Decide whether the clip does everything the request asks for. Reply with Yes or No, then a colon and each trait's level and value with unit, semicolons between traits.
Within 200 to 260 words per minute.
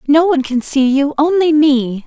Yes: fast, 205 wpm